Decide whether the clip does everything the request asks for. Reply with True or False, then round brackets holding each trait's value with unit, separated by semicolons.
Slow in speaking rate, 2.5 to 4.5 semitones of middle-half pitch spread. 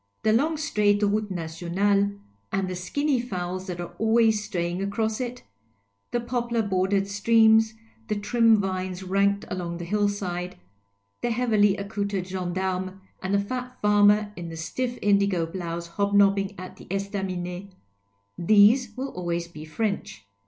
False (145 wpm; 2.9 semitones)